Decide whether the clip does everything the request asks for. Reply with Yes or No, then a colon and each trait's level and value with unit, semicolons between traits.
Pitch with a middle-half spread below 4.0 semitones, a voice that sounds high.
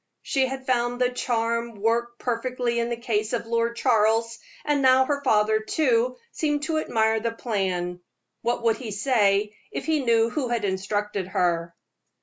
Yes: average, 2.8 semitones; high, 230 Hz